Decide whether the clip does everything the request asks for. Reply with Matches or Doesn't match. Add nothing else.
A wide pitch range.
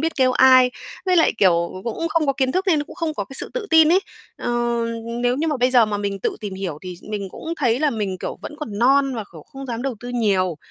Matches